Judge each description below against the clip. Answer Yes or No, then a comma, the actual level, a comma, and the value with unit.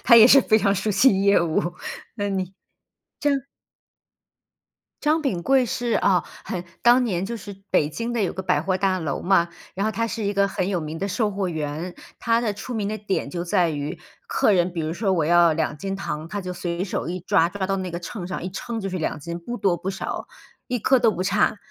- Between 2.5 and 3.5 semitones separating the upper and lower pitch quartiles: No, average, 4.0 semitones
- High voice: Yes, high, 195 Hz